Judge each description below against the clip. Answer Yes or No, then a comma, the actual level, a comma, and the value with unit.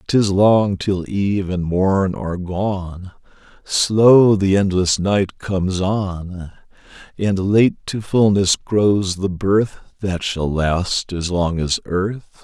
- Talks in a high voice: No, very low, 95 Hz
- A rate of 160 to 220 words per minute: No, slow, 135 wpm